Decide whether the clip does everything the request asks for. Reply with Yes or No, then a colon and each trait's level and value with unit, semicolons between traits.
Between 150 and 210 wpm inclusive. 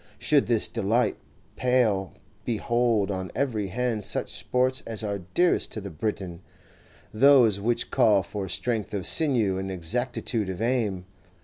No: average, 140 wpm